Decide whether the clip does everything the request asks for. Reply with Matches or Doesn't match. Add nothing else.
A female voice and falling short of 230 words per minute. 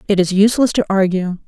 Matches